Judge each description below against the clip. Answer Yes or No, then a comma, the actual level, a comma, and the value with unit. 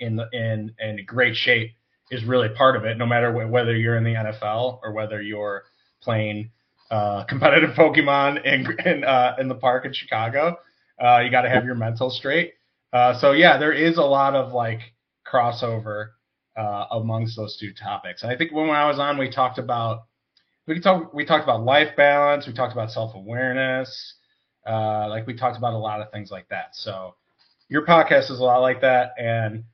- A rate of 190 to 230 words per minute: Yes, average, 200 wpm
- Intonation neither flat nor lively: Yes, average, 3.0 semitones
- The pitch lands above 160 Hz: No, low, 120 Hz